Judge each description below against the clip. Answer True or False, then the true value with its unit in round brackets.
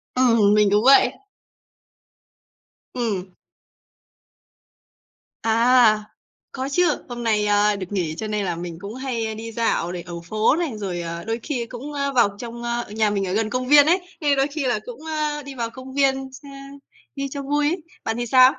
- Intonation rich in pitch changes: False (4.6 semitones)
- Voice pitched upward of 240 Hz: False (235 Hz)